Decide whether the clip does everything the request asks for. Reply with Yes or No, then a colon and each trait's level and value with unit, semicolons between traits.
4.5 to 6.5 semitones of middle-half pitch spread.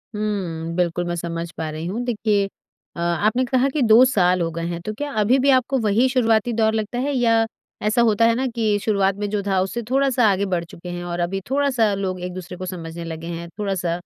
Yes: average, 5.0 semitones